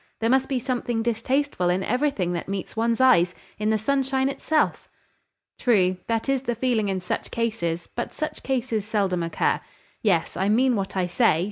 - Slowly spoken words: No, average, 175 wpm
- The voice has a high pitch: Yes, high, 225 Hz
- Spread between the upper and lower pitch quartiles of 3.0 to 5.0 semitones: No, wide, 5.5 semitones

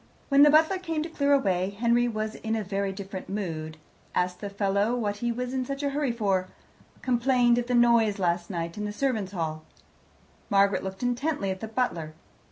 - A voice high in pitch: Yes, high, 215 Hz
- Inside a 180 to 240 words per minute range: Yes, average, 195 wpm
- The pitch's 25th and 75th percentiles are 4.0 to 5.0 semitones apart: Yes, average, 4.6 semitones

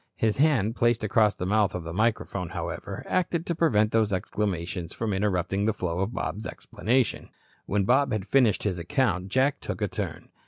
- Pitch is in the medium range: No, low, 105 Hz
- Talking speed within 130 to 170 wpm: No, average, 185 wpm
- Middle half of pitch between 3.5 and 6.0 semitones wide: Yes, average, 4.0 semitones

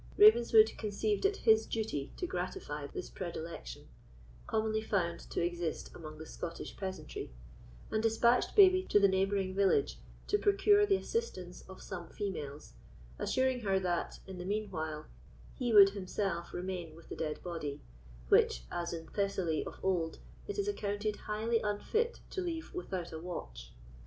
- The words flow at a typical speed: Yes, average, 155 wpm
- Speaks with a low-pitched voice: No, high, 195 Hz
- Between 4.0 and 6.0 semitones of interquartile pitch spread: Yes, wide, 5.4 semitones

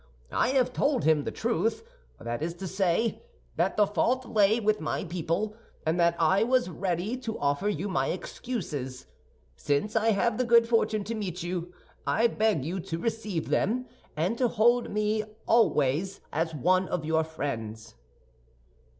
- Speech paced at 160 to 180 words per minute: Yes, average, 165 wpm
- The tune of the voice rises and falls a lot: Yes, wide, 5.7 semitones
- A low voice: No, high, 195 Hz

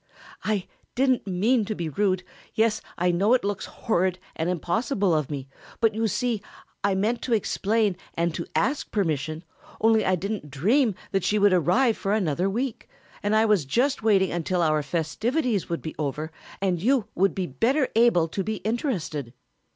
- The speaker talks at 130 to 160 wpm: No, average, 175 wpm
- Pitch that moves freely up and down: No, average, 4.6 semitones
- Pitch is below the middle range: No, high, 200 Hz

